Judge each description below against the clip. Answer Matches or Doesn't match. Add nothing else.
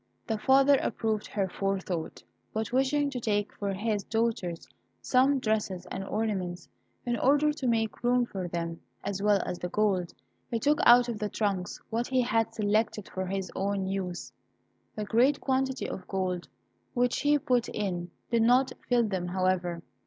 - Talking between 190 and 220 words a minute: Doesn't match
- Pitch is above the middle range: Matches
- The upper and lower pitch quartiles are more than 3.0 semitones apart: Matches